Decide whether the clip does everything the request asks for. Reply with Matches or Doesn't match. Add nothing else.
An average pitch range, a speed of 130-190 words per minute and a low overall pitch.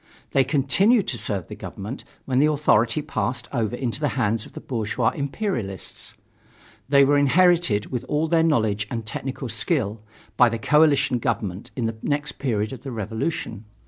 Matches